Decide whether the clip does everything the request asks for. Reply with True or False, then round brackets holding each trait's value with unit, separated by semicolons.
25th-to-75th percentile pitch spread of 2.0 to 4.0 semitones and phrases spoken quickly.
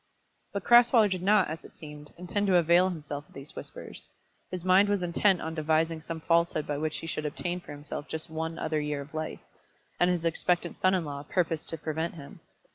True (2.7 semitones; 210 wpm)